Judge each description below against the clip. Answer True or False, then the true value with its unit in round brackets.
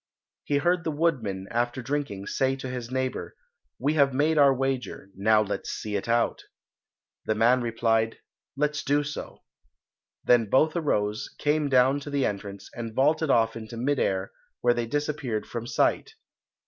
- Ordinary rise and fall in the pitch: True (4.2 semitones)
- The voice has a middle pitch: False (125 Hz)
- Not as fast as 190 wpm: True (160 wpm)